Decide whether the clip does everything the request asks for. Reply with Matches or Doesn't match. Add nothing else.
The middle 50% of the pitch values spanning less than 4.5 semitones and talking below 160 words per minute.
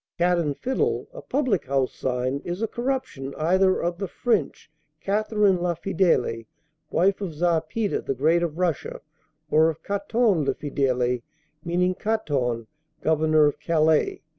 Doesn't match